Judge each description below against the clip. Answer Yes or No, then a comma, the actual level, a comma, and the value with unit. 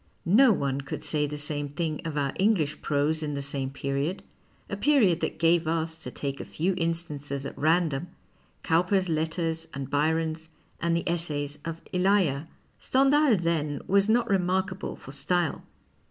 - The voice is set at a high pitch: No, medium, 160 Hz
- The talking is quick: No, average, 165 wpm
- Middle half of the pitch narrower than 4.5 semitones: Yes, average, 3.8 semitones